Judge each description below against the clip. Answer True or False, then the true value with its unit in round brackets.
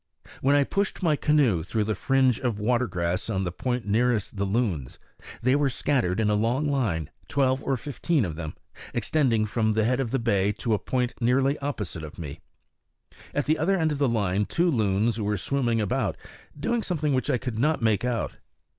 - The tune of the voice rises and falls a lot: False (5.0 semitones)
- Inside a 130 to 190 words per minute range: False (200 wpm)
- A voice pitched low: True (120 Hz)